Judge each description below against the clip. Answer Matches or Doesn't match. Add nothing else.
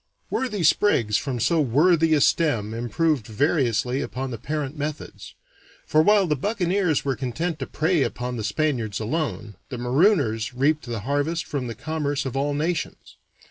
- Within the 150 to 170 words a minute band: Matches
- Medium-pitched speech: Matches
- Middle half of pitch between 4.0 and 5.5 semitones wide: Matches